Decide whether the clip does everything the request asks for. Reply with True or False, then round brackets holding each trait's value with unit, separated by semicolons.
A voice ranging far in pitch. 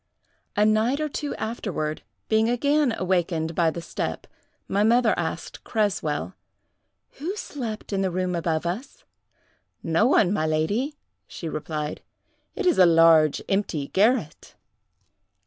True (6.2 semitones)